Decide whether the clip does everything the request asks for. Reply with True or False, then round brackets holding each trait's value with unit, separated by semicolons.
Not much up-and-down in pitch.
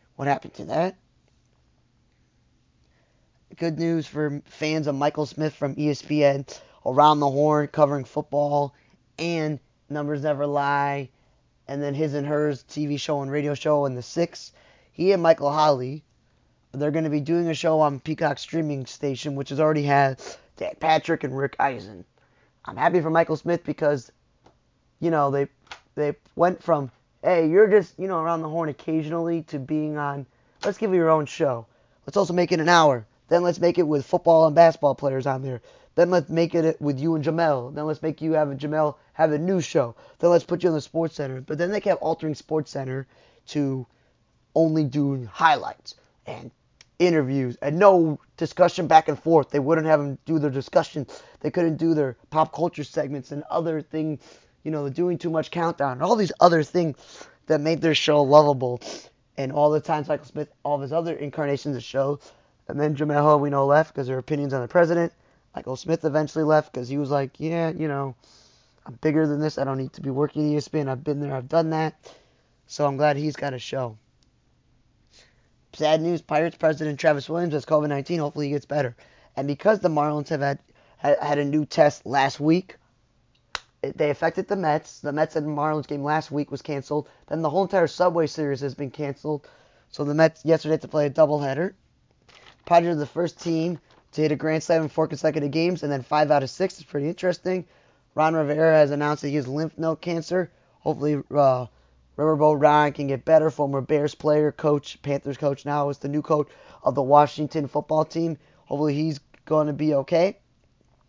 True (2.2 semitones)